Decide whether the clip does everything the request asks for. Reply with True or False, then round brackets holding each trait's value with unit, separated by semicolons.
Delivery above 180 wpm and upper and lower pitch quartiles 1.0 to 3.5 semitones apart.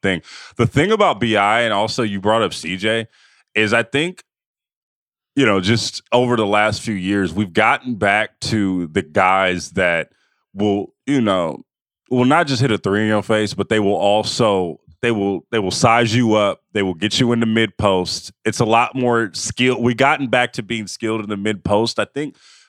True (205 wpm; 2.8 semitones)